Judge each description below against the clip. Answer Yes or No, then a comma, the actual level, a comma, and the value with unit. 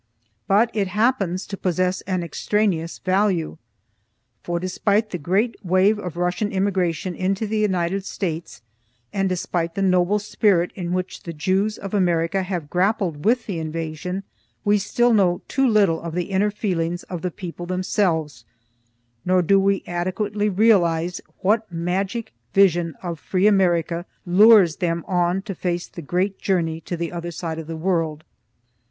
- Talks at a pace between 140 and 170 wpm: Yes, average, 155 wpm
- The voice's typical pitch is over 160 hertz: Yes, medium, 185 Hz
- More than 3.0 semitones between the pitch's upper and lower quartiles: No, average, 2.7 semitones